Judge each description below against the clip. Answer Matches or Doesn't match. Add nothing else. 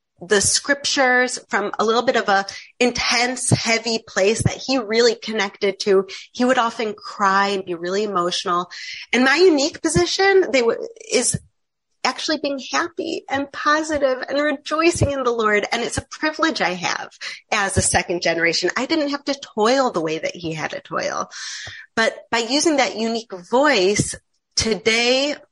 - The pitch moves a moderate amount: Doesn't match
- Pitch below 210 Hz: Doesn't match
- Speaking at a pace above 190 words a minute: Doesn't match